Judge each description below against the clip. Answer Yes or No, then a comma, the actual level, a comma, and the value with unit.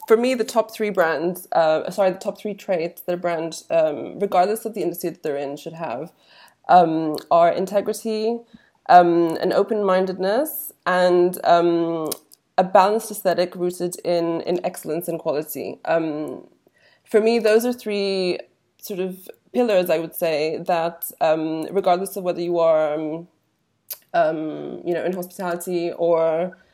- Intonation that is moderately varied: Yes, average, 3.8 semitones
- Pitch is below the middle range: No, medium, 180 Hz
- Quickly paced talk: No, average, 155 wpm